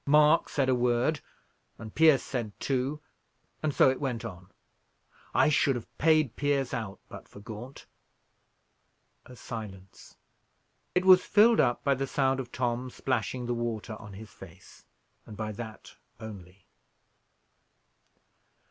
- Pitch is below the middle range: Yes, low, 125 Hz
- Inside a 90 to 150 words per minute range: Yes, average, 140 wpm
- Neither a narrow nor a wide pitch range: Yes, average, 4.1 semitones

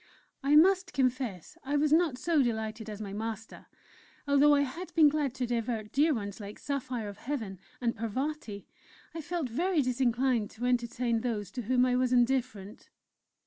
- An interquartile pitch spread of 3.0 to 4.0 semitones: No, average, 4.4 semitones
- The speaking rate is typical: Yes, average, 170 wpm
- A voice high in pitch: Yes, very high, 250 Hz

